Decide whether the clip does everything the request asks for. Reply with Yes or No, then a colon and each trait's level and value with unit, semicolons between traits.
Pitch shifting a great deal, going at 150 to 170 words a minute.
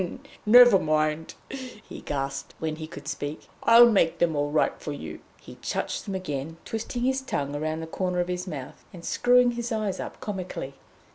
No: wide, 6.2 semitones; average, 185 wpm